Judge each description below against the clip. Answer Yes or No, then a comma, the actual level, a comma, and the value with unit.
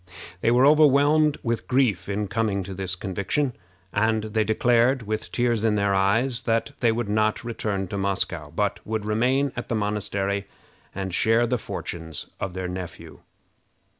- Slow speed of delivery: No, average, 165 wpm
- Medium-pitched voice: No, low, 110 Hz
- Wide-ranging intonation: No, average, 3.4 semitones